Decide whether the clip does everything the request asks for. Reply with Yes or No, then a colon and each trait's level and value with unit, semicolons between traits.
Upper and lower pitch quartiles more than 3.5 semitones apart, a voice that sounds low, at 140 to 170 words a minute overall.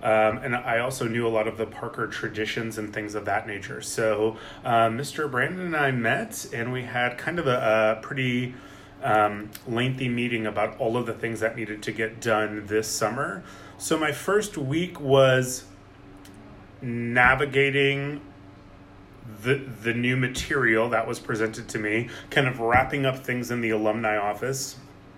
No: average, 3.1 semitones; low, 115 Hz; average, 165 wpm